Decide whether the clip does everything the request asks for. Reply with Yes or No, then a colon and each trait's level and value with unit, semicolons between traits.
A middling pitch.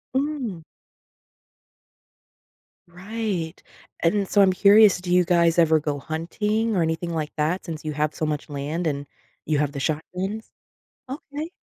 Yes: medium, 170 Hz